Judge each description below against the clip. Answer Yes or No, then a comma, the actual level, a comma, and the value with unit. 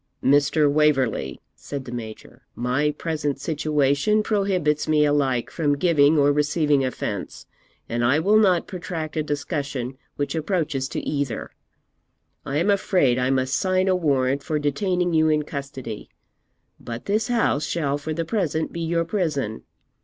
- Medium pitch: Yes, medium, 150 Hz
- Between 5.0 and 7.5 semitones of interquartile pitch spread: No, average, 3.4 semitones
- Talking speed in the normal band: Yes, average, 150 wpm